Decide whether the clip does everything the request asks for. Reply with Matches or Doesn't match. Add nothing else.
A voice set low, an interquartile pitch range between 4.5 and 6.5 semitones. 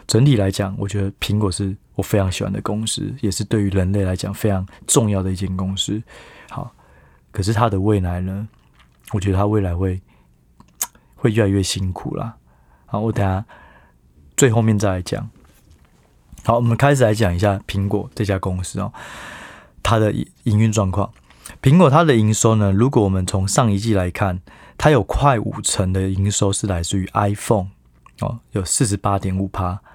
Doesn't match